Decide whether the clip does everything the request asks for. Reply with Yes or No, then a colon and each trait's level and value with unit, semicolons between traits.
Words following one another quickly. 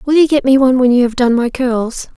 Yes: fast, 300 wpm